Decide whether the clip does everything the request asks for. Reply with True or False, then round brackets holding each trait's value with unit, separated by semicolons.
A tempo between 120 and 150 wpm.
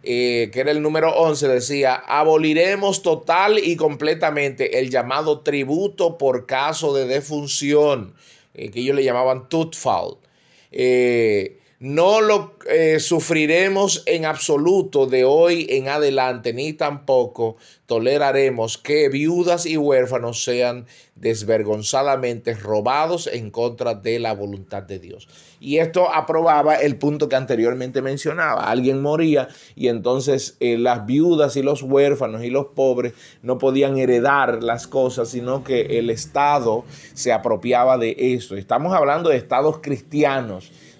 True (135 wpm)